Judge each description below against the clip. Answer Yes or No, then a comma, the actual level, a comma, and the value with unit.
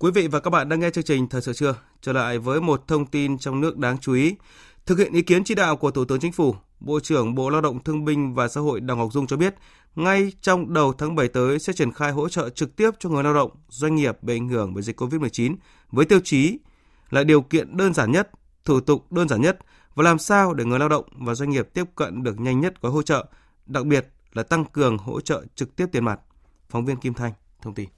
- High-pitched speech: No, medium, 145 Hz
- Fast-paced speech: Yes, fast, 265 wpm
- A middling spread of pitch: Yes, average, 4.3 semitones